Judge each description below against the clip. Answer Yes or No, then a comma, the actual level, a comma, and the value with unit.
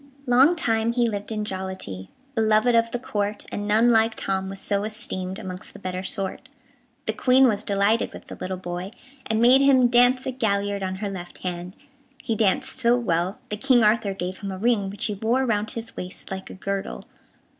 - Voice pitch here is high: Yes, high, 210 Hz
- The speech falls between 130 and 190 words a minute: No, average, 200 wpm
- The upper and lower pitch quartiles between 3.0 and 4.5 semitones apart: Yes, average, 3.6 semitones